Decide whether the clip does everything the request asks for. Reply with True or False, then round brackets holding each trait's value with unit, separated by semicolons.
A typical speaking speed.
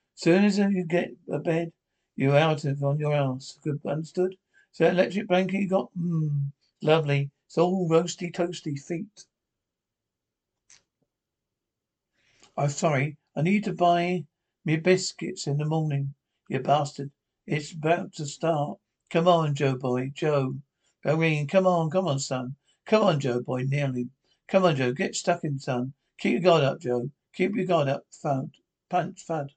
True (160 wpm)